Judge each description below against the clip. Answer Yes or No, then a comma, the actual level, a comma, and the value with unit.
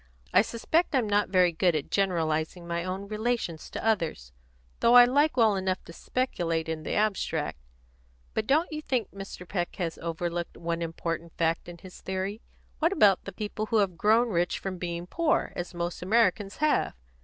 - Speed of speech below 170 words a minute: No, average, 180 wpm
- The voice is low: No, medium, 185 Hz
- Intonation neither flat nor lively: Yes, average, 4.5 semitones